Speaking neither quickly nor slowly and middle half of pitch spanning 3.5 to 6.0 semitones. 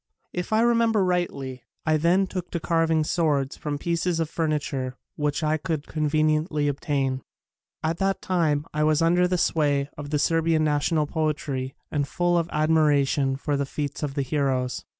No: average, 170 wpm; average, 2.7 semitones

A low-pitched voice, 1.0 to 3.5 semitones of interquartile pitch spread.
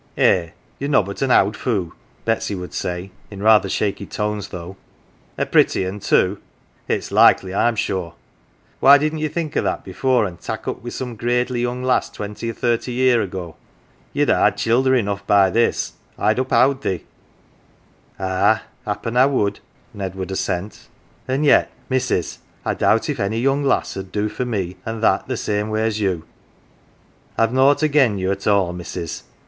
No: low, 105 Hz; average, 4.6 semitones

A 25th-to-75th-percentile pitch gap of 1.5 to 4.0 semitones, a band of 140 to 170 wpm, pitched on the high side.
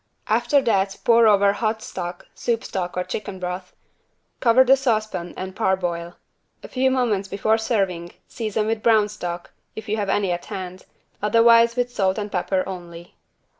Yes: average, 3.7 semitones; average, 165 wpm; high, 205 Hz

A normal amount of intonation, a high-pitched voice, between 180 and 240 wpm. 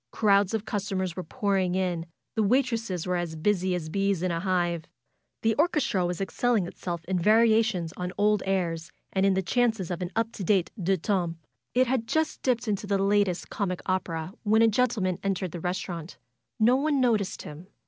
Yes: average, 3.6 semitones; high, 195 Hz; average, 195 wpm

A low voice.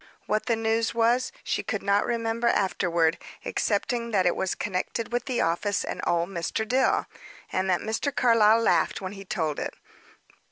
No: high, 215 Hz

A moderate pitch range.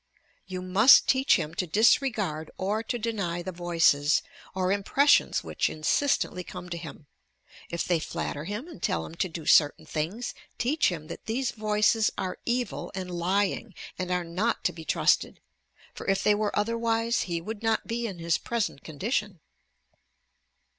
Yes: average, 4.9 semitones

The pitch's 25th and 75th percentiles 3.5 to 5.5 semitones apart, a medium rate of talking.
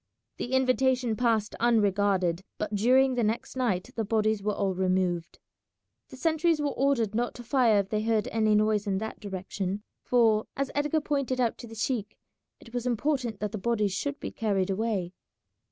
Yes: average, 3.8 semitones; average, 180 wpm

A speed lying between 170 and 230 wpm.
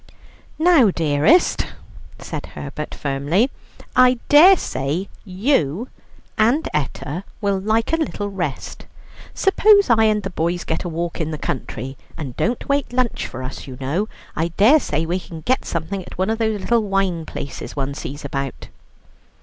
No: average, 160 wpm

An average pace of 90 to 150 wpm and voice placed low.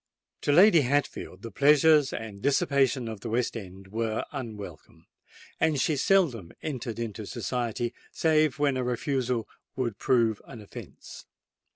Yes: average, 140 wpm; low, 120 Hz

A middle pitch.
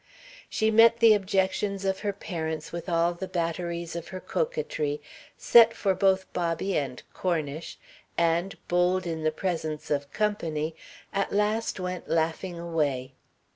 Yes: medium, 180 Hz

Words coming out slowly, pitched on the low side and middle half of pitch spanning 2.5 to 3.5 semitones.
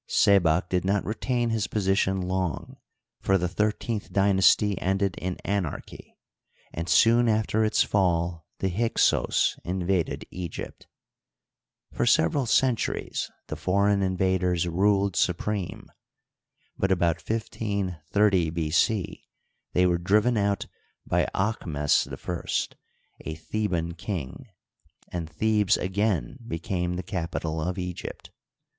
Yes: slow, 115 wpm; very low, 95 Hz; average, 3.0 semitones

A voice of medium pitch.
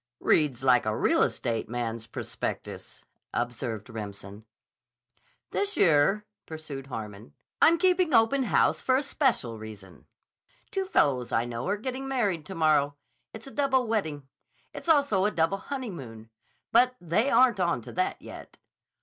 Yes: medium, 160 Hz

